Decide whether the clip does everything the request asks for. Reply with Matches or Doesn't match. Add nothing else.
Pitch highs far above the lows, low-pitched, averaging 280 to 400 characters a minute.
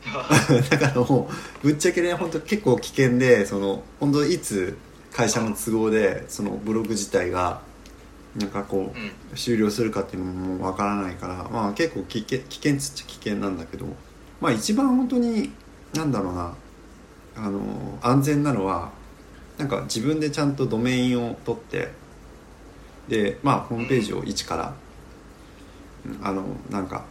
Matches